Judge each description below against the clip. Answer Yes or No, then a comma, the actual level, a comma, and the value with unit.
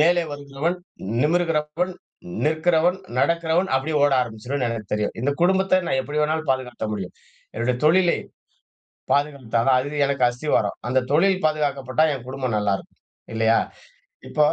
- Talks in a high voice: No, medium, 145 Hz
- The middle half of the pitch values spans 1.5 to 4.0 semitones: No, average, 4.4 semitones